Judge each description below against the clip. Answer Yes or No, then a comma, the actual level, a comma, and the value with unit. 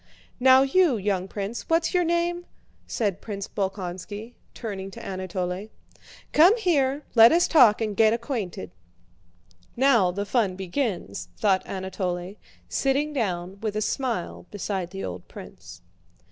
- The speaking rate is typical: No, slow, 130 wpm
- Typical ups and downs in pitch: No, wide, 5.9 semitones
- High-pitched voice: Yes, high, 210 Hz